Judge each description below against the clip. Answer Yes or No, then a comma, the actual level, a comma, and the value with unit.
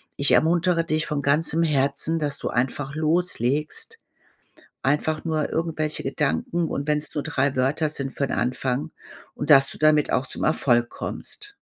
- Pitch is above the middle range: No, medium, 150 Hz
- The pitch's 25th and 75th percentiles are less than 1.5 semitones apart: No, narrow, 2.6 semitones